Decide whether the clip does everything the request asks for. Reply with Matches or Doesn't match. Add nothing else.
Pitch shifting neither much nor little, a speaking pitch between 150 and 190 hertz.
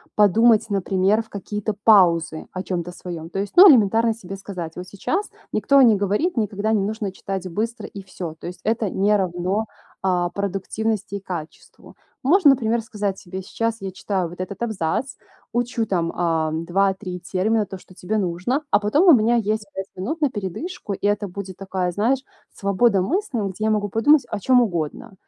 Doesn't match